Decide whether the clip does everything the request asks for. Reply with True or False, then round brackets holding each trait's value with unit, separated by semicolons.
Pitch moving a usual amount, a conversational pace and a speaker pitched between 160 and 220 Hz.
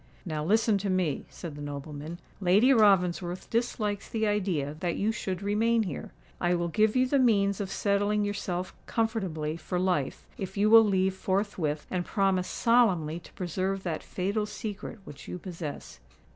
True (3.3 semitones; 165 wpm; 190 Hz)